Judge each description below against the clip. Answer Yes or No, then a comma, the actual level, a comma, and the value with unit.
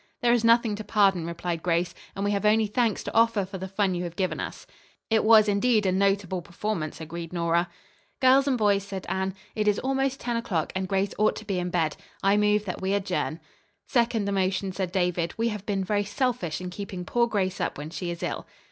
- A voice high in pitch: Yes, high, 195 Hz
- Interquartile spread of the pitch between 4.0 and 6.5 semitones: No, average, 3.1 semitones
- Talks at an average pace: No, fast, 225 wpm